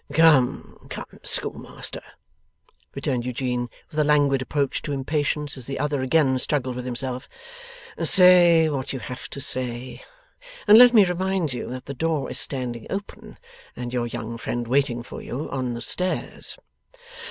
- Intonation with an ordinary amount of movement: Yes, average, 3.6 semitones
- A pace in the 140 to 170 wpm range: Yes, average, 155 wpm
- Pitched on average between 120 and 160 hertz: Yes, low, 135 Hz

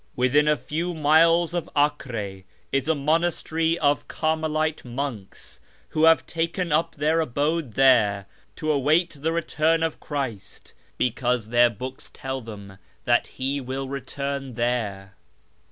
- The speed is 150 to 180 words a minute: No, slow, 135 wpm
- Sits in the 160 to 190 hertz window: No, medium, 140 Hz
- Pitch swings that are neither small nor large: Yes, average, 4.4 semitones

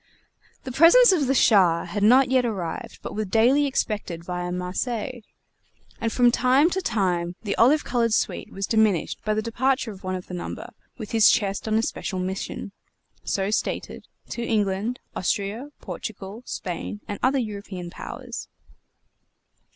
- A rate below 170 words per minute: Yes, average, 160 wpm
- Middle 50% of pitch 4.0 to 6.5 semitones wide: Yes, average, 4.6 semitones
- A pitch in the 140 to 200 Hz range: No, high, 215 Hz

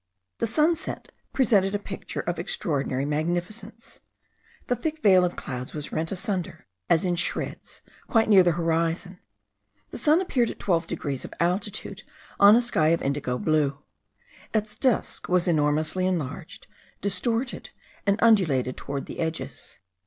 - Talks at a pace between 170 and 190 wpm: No, average, 145 wpm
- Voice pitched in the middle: Yes, medium, 180 Hz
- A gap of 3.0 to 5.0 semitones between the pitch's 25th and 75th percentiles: No, wide, 5.5 semitones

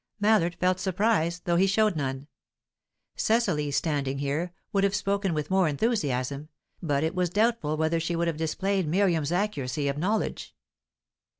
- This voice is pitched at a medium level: Yes, medium, 170 Hz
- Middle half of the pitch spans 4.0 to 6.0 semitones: Yes, average, 4.8 semitones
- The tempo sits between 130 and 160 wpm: Yes, average, 155 wpm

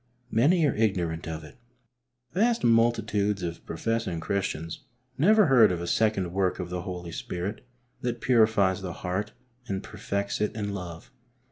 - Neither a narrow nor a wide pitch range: Yes, average, 4.3 semitones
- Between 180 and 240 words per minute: No, average, 150 wpm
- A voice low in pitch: Yes, low, 100 Hz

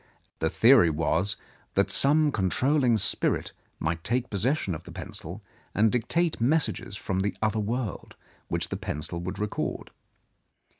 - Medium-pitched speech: No, low, 105 Hz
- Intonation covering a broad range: Yes, wide, 5.7 semitones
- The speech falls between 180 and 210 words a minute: No, average, 145 wpm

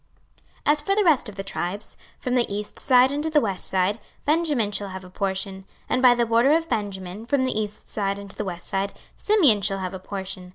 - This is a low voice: No, high, 210 Hz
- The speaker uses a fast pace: Yes, fast, 235 wpm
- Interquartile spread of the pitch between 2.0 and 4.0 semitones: No, average, 5.1 semitones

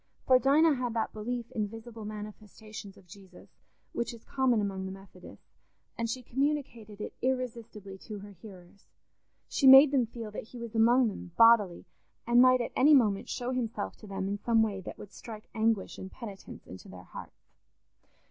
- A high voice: Yes, high, 225 Hz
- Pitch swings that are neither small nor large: Yes, average, 3.4 semitones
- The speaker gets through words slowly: No, average, 180 wpm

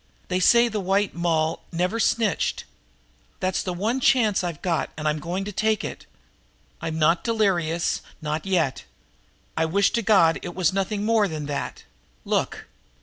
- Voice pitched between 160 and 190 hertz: Yes, medium, 185 Hz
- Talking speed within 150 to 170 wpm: Yes, average, 160 wpm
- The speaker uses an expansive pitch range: No, average, 4.3 semitones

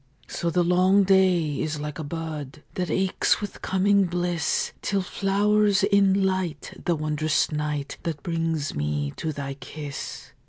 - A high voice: No, medium, 170 Hz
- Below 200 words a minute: Yes, average, 150 wpm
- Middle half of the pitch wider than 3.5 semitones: Yes, average, 4.1 semitones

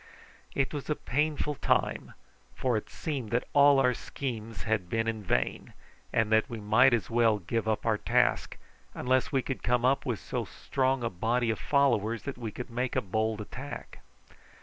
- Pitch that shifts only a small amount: No, average, 3.2 semitones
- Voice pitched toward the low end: Yes, low, 120 Hz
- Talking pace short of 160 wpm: No, average, 180 wpm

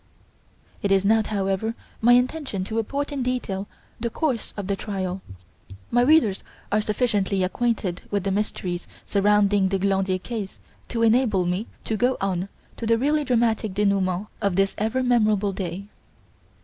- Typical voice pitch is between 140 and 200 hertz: No, high, 210 Hz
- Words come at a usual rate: Yes, average, 155 wpm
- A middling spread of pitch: Yes, average, 3.3 semitones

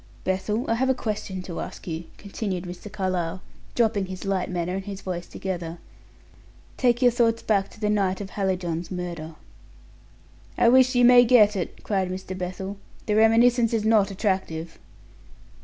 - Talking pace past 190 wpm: No, average, 165 wpm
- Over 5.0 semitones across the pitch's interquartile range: No, average, 3.6 semitones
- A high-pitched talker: Yes, high, 195 Hz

